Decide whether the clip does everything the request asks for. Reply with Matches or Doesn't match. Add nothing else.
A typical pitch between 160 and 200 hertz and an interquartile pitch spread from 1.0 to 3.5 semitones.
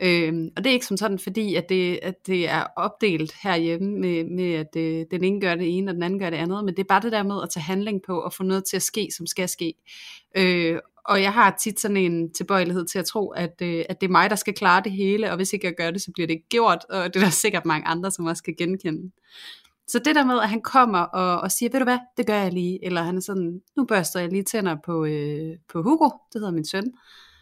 Matches